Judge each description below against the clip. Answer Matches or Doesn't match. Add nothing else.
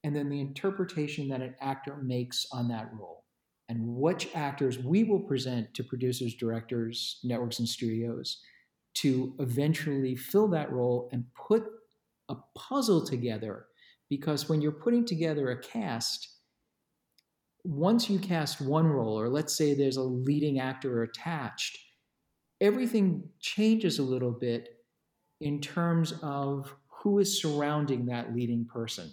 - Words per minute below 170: Matches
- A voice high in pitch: Doesn't match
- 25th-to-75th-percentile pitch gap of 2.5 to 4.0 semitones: Doesn't match